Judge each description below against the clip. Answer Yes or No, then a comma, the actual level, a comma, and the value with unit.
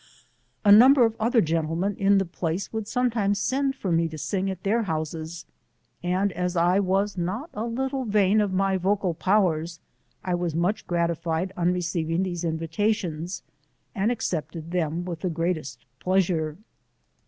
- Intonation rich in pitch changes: No, average, 3.6 semitones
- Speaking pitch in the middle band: Yes, medium, 180 Hz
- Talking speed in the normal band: Yes, average, 155 wpm